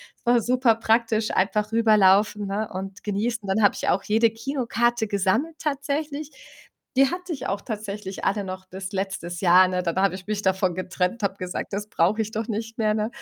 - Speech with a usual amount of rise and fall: Yes, average, 3.1 semitones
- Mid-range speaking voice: No, high, 210 Hz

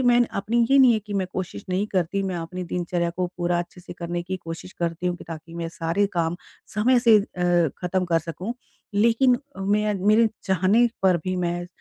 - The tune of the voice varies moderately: Yes, average, 3.2 semitones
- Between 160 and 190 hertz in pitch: Yes, medium, 185 Hz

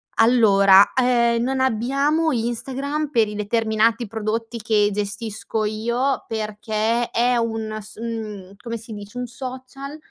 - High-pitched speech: Yes, high, 230 Hz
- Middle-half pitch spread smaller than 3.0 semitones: Yes, narrow, 2.6 semitones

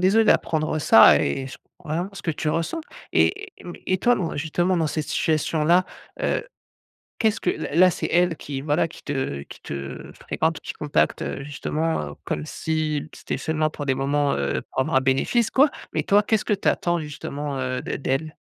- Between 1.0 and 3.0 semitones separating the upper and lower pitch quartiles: No, average, 4.0 semitones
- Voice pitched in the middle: Yes, medium, 155 Hz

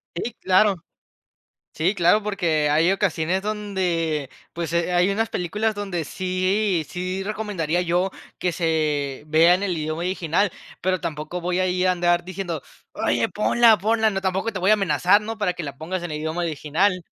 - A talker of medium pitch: Yes, medium, 180 Hz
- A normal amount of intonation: Yes, average, 3.1 semitones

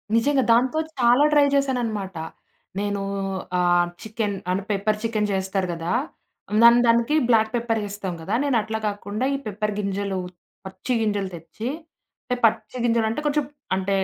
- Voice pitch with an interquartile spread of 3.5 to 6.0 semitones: No, average, 3.1 semitones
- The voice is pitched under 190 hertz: No, high, 215 Hz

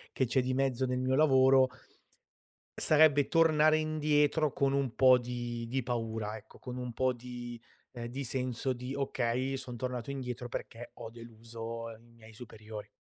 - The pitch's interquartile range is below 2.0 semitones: No, narrow, 2.4 semitones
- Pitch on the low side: Yes, low, 125 Hz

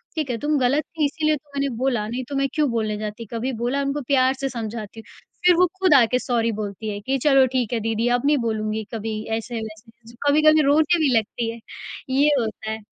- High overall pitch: Yes, high, 245 Hz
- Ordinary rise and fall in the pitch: Yes, average, 4.1 semitones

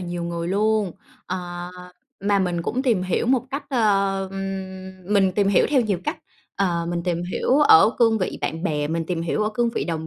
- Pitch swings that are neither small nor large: Yes, average, 3.9 semitones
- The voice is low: No, high, 190 Hz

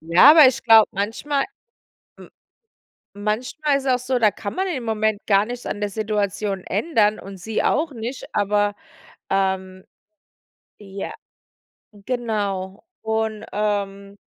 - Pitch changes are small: No, average, 3.3 semitones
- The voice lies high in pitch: Yes, high, 210 Hz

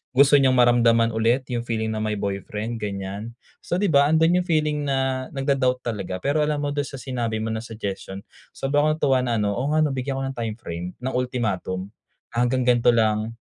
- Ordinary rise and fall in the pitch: Yes, average, 4.0 semitones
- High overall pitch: No, low, 125 Hz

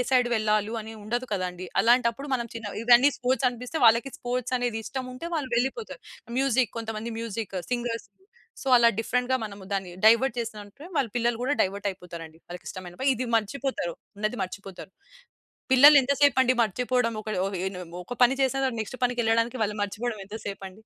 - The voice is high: Yes, high, 230 Hz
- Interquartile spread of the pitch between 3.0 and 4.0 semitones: Yes, average, 3.5 semitones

